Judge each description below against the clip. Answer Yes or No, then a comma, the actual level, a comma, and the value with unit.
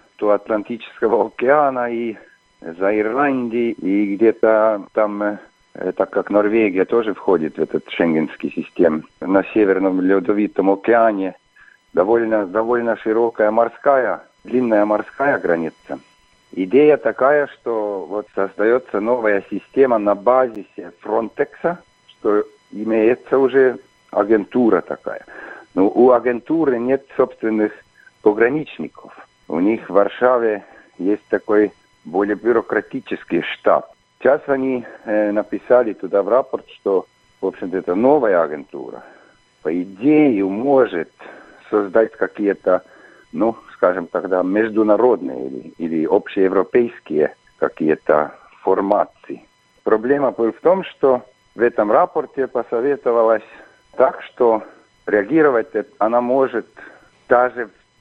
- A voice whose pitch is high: No, low, 110 Hz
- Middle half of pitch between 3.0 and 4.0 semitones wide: Yes, average, 3.3 semitones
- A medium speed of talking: No, slow, 105 wpm